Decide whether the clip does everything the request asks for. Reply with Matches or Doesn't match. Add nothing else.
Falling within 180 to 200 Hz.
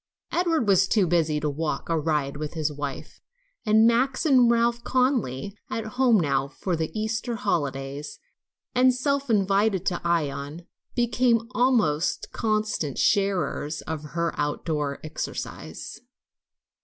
Matches